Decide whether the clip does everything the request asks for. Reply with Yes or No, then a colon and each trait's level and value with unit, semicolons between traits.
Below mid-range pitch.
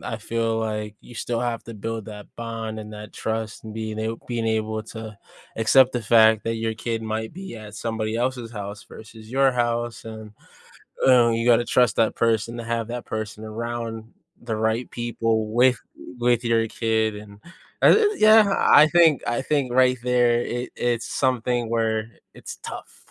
Yes: low, 115 Hz